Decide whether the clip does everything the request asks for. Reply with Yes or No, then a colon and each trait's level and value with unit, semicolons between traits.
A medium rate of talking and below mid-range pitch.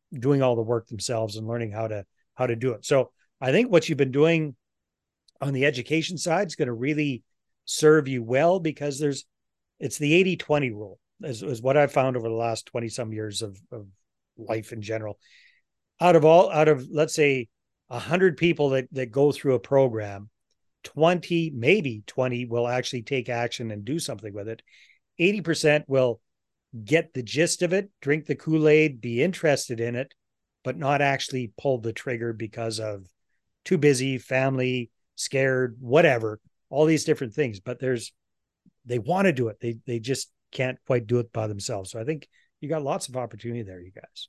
Yes: average, 185 wpm; low, 130 Hz